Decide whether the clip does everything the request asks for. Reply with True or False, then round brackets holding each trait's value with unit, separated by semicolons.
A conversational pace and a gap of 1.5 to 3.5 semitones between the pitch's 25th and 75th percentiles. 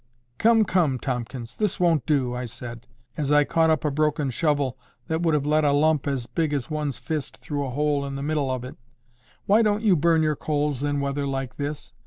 False (220 wpm; 2.6 semitones)